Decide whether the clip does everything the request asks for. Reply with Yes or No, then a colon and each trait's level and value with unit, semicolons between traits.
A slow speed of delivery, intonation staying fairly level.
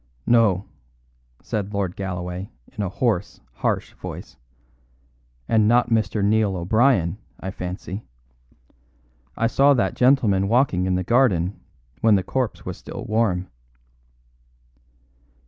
No: slow, 115 wpm; average, 3.8 semitones